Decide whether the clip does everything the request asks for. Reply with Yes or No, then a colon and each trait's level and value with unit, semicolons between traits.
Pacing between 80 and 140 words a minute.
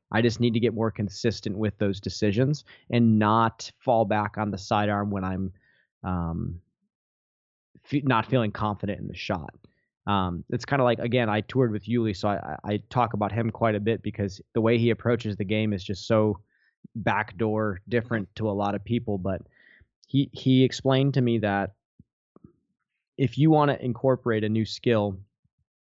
No: average, 180 wpm